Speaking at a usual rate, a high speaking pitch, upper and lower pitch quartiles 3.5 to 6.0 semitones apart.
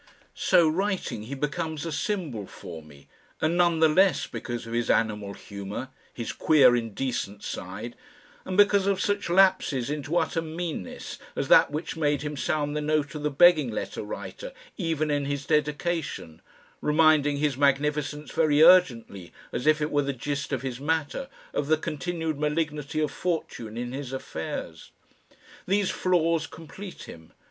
No: average, 160 wpm; medium, 150 Hz; average, 3.8 semitones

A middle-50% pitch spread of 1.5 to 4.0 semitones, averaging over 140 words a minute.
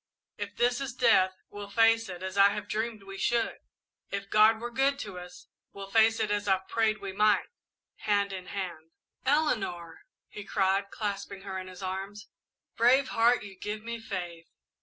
Yes: average, 2.9 semitones; average, 180 wpm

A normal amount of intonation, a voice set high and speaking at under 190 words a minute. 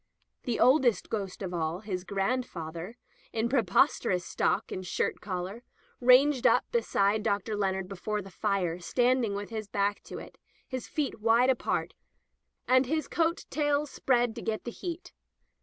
Yes: average, 4.7 semitones; high, 220 Hz; average, 155 wpm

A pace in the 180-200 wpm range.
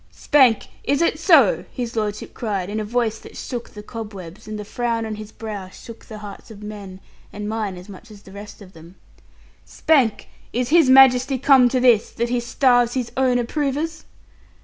Yes: average, 195 wpm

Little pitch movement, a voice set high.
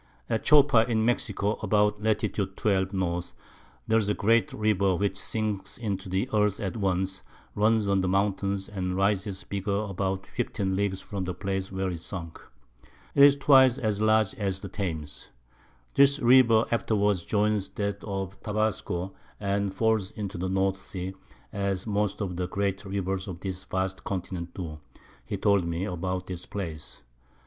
No: narrow, 2.1 semitones; low, 100 Hz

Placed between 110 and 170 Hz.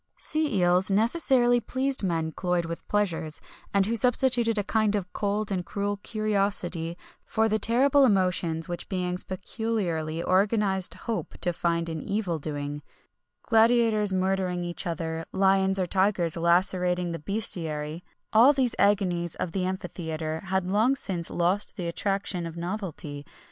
No: high, 190 Hz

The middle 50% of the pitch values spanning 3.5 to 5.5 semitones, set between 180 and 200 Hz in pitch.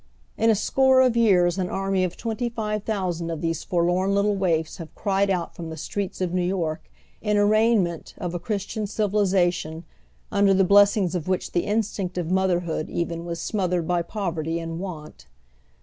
No: average, 3.1 semitones; medium, 185 Hz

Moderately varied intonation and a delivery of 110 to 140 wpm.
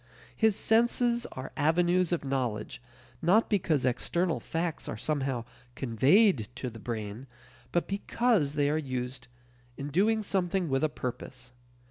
No: wide, 6.8 semitones; slow, 135 wpm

